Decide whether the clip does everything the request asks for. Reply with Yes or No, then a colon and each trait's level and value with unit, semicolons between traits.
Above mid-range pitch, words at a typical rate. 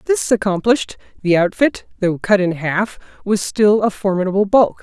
Yes: high, 205 Hz; average, 160 wpm